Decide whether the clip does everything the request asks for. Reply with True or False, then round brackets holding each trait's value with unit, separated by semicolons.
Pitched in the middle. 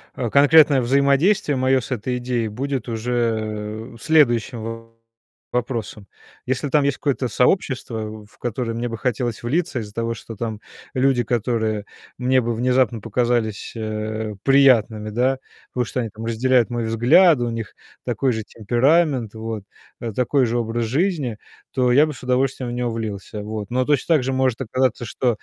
False (120 Hz)